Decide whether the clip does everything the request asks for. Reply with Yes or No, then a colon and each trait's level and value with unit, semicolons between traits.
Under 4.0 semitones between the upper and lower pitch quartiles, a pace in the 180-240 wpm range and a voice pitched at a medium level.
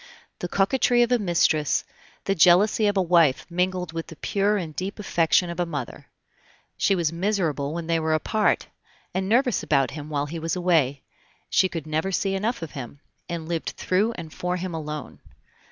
Yes: average, 3.6 semitones; average, 185 wpm; medium, 175 Hz